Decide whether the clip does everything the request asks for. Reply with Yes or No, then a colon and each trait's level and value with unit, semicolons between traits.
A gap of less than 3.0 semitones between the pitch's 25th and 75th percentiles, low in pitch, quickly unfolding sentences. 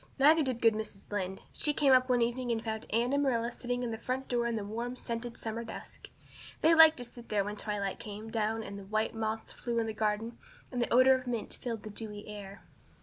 No: narrow, 2.4 semitones; high, 230 Hz; fast, 250 wpm